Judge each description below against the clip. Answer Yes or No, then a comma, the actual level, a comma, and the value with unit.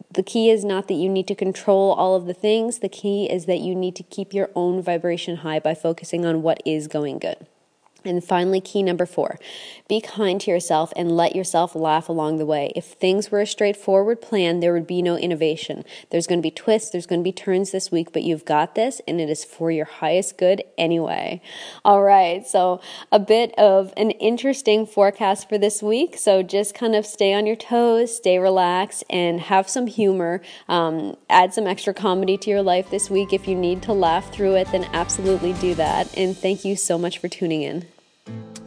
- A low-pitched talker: No, medium, 185 Hz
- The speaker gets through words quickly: Yes, fast, 215 wpm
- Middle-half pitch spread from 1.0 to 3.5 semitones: Yes, average, 2.9 semitones